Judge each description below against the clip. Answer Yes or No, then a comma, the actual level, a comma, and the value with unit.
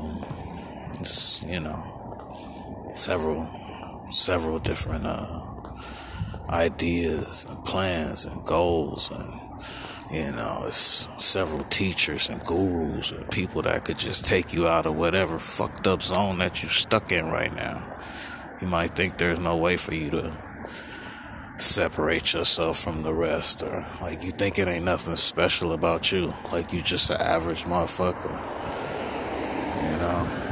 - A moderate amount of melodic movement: No, narrow, 2.1 semitones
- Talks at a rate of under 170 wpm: Yes, average, 140 wpm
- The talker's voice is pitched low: Yes, very low, 85 Hz